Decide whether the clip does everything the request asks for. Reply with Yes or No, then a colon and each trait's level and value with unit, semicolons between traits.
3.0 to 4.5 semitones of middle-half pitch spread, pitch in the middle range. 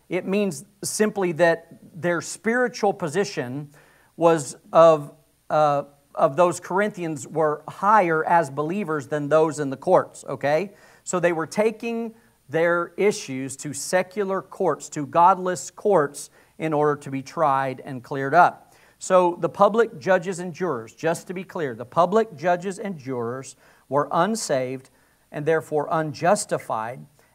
Yes: average, 4.2 semitones; medium, 165 Hz